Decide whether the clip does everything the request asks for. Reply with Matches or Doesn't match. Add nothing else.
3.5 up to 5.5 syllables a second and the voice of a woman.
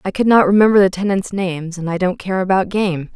Doesn't match